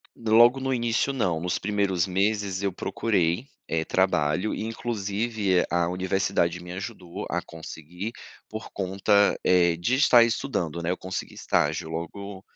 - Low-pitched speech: Yes, very low, 95 Hz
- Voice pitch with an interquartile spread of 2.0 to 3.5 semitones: No, average, 4.0 semitones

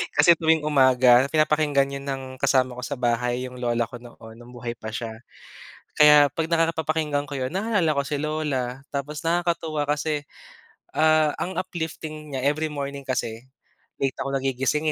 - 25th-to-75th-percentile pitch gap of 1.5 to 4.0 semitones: Yes, average, 3.4 semitones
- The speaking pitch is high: No, medium, 140 Hz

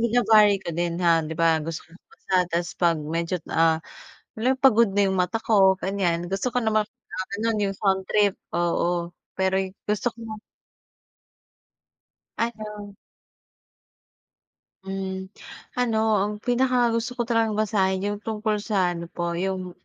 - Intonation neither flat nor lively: Yes, average, 4.0 semitones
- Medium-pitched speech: No, high, 195 Hz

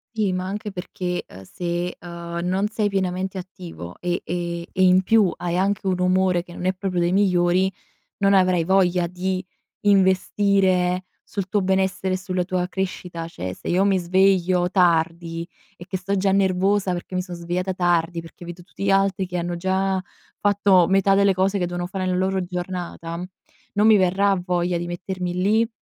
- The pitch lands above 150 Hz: Yes, medium, 185 Hz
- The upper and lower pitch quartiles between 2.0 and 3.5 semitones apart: No, narrow, 1.6 semitones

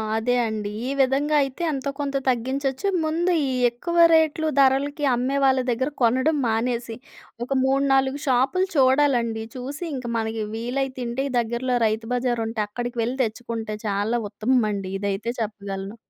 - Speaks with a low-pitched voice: No, very high, 250 Hz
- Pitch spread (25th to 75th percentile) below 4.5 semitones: Yes, average, 3.3 semitones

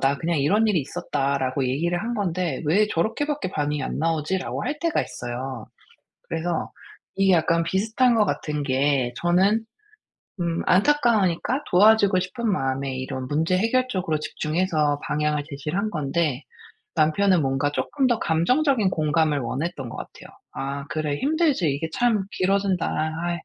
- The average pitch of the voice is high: No, medium, 170 Hz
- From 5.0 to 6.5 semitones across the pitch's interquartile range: Yes, wide, 5.6 semitones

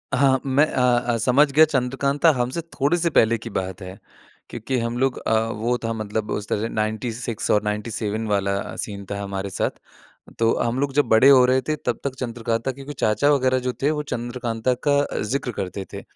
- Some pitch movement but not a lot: Yes, average, 3.8 semitones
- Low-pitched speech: Yes, low, 120 Hz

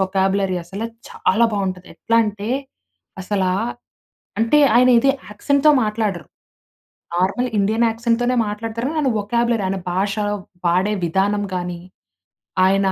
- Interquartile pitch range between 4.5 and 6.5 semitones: No, average, 3.3 semitones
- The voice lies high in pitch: Yes, high, 205 Hz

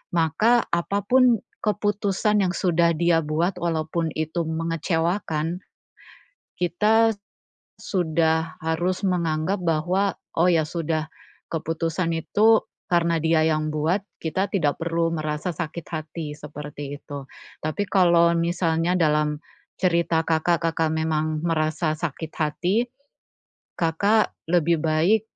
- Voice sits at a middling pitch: Yes, medium, 165 Hz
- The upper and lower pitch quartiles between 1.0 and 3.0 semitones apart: Yes, narrow, 2.4 semitones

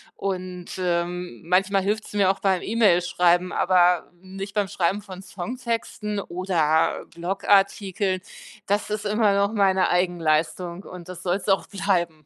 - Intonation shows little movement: Yes, narrow, 2.2 semitones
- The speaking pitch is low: No, medium, 185 Hz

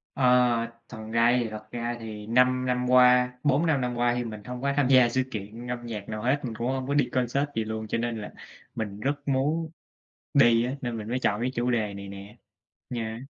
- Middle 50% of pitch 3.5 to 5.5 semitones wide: No, narrow, 2.5 semitones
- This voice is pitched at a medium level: No, low, 120 Hz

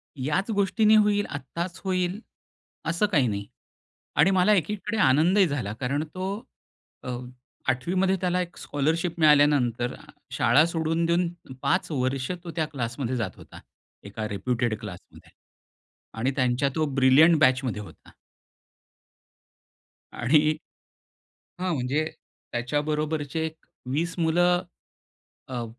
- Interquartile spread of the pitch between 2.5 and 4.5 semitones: No, wide, 5.4 semitones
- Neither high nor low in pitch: Yes, medium, 155 Hz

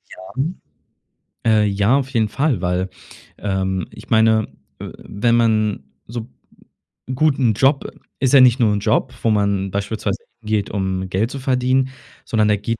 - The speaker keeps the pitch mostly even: No, average, 3.9 semitones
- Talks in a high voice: No, low, 110 Hz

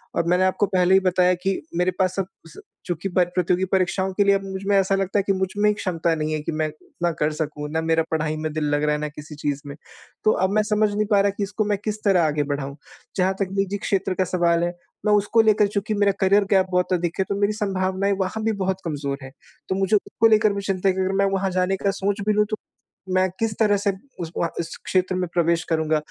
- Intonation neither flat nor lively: Yes, average, 3.1 semitones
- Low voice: No, medium, 185 Hz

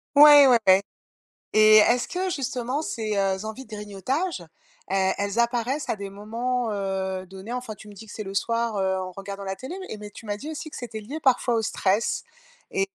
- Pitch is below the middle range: No, high, 220 Hz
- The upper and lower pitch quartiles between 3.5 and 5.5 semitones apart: Yes, average, 4.2 semitones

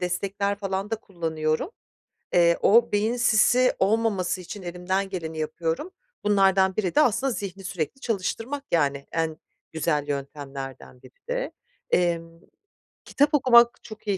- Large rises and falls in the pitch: No, average, 5.0 semitones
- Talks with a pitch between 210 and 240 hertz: No, high, 190 Hz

